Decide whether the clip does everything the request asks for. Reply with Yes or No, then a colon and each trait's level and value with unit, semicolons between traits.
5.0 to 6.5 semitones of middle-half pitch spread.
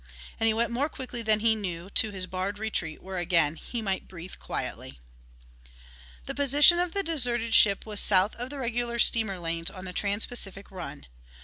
No: average, 4.3 semitones